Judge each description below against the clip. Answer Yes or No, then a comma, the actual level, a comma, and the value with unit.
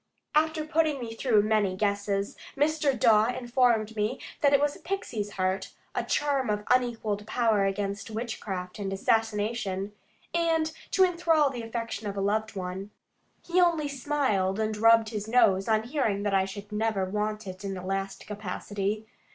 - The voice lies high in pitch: Yes, high, 215 Hz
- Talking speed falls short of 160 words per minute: No, average, 165 wpm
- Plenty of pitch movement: No, average, 4.3 semitones